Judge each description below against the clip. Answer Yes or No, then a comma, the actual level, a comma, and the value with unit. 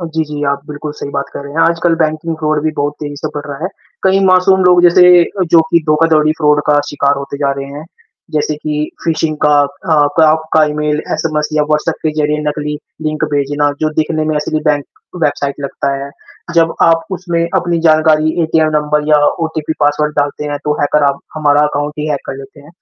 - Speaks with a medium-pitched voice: Yes, medium, 150 Hz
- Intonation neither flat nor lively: No, narrow, 1.5 semitones